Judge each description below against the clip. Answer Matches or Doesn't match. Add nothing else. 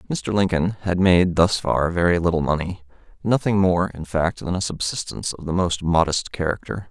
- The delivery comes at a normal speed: Matches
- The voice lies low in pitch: Matches